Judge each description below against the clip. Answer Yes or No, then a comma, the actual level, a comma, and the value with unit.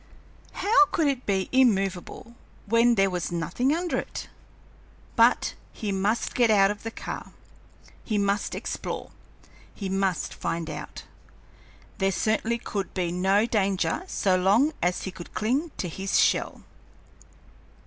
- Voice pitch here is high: Yes, high, 200 Hz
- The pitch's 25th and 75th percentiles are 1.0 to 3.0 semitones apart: No, average, 3.7 semitones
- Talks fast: No, average, 140 wpm